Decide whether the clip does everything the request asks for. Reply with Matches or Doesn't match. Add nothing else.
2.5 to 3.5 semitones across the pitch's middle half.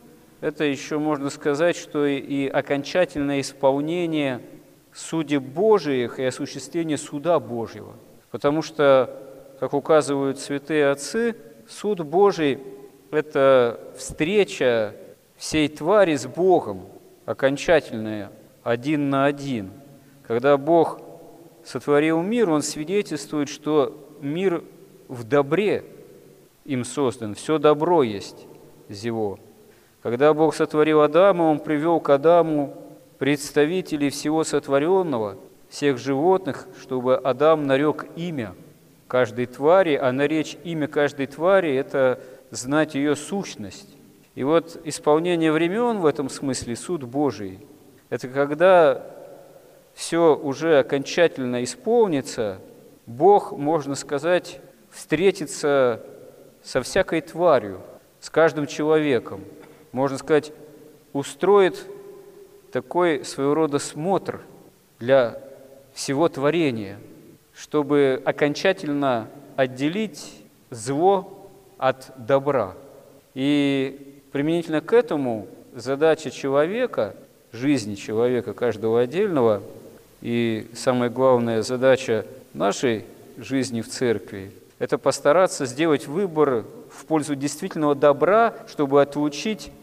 Matches